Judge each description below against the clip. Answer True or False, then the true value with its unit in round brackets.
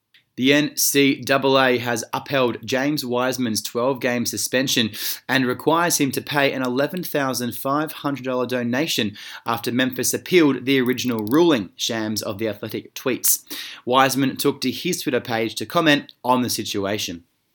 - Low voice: True (130 Hz)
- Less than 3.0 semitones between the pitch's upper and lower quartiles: True (2.6 semitones)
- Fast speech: False (135 wpm)